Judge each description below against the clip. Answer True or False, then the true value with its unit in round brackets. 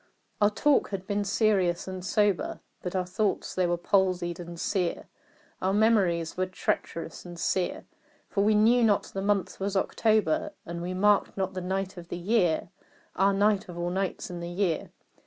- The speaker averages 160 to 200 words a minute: True (180 wpm)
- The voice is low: False (190 Hz)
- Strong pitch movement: False (2.7 semitones)